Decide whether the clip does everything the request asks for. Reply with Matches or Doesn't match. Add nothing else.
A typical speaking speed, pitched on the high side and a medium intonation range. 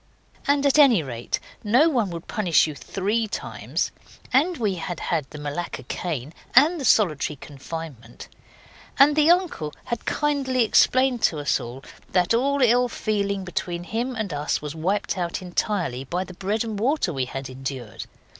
Doesn't match